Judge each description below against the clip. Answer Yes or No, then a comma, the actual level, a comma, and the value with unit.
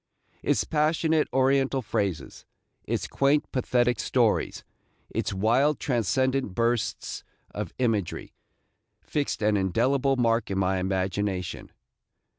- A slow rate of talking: Yes, slow, 100 wpm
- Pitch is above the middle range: No, low, 120 Hz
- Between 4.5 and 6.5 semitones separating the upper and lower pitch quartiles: Yes, average, 5.1 semitones